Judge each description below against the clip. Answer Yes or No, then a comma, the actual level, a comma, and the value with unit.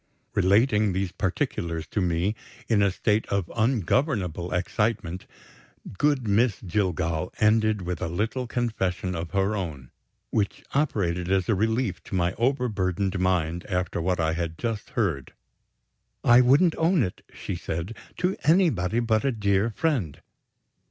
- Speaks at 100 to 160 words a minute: Yes, average, 140 wpm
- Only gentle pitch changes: No, average, 4.4 semitones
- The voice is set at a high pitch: No, low, 100 Hz